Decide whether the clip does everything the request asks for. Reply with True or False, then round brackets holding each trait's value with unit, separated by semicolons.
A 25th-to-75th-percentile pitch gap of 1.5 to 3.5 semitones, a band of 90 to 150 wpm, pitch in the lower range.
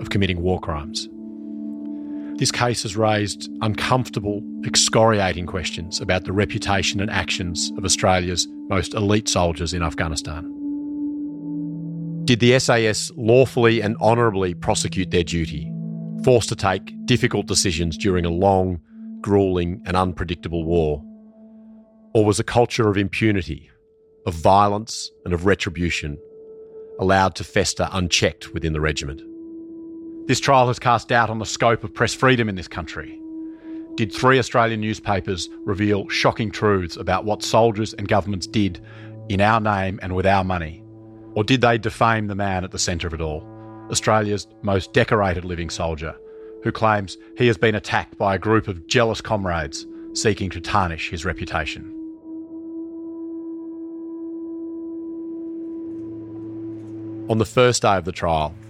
False (5.3 semitones; 140 wpm; 110 Hz)